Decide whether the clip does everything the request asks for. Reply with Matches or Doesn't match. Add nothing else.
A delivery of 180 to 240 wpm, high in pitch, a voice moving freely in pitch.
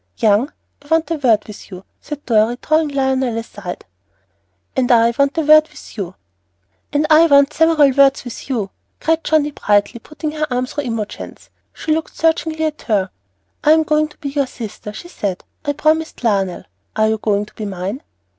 Matches